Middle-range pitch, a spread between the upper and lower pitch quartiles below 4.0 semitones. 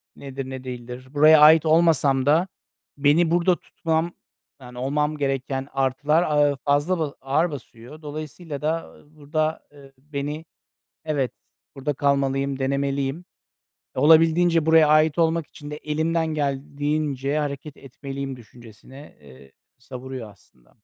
Yes: medium, 145 Hz; narrow, 2.6 semitones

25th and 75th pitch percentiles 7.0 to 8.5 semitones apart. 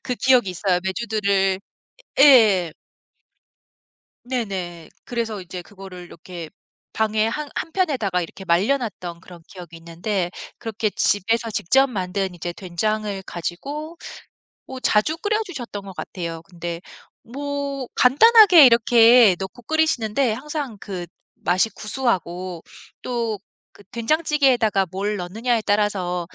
No: wide, 5.6 semitones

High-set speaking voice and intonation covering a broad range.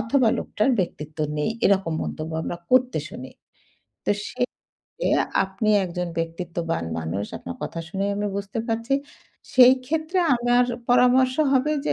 Yes: high, 210 Hz; wide, 6.7 semitones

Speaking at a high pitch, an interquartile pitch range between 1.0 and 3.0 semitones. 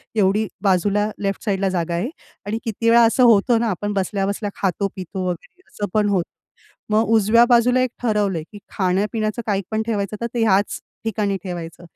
Yes: high, 205 Hz; narrow, 2.5 semitones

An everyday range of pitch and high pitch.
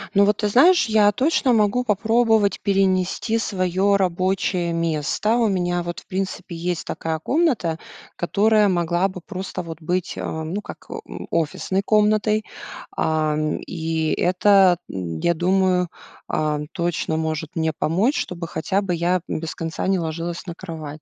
No: average, 3.8 semitones; medium, 180 Hz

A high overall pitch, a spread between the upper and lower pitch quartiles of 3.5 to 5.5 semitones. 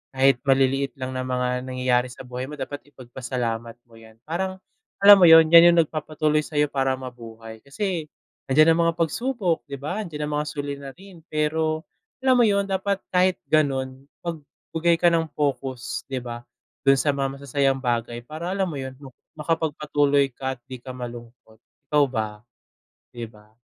No: medium, 140 Hz; average, 4.1 semitones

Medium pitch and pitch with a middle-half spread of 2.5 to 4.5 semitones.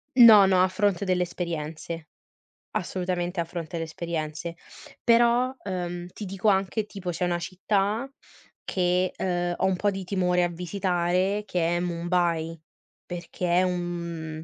No: medium, 180 Hz; narrow, 1.9 semitones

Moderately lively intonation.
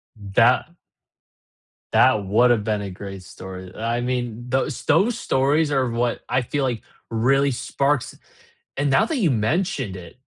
Yes: average, 4.4 semitones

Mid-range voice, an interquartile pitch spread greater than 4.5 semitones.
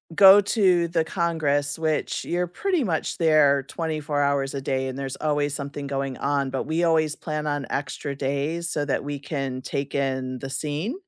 No: medium, 145 Hz; average, 2.8 semitones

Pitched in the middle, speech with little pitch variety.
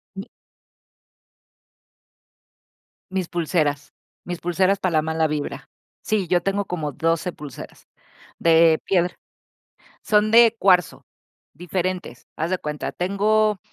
No: medium, 180 Hz; average, 3.4 semitones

